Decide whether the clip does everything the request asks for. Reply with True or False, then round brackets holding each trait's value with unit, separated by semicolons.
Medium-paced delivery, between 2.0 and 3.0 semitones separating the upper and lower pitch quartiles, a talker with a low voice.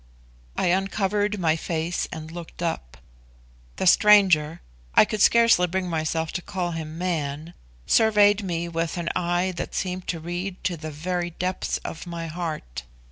False (155 wpm; 2.5 semitones; 175 Hz)